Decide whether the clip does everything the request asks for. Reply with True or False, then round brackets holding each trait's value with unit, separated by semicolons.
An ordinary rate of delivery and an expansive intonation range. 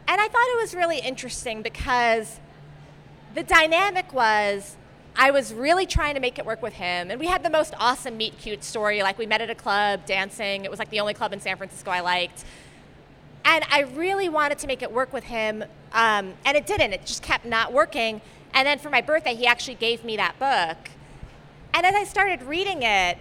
False (215 wpm; 6.6 semitones)